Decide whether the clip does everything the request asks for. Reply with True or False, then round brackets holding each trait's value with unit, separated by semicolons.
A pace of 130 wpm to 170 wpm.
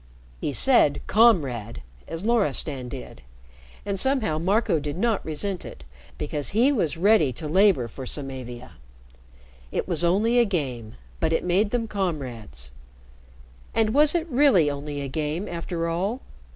True (145 wpm)